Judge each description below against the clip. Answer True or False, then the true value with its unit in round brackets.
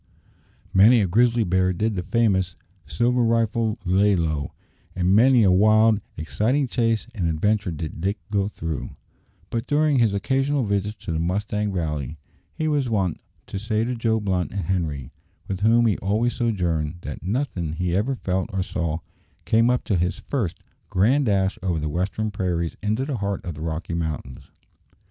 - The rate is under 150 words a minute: False (170 wpm)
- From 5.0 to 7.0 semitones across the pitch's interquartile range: False (4.6 semitones)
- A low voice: True (100 Hz)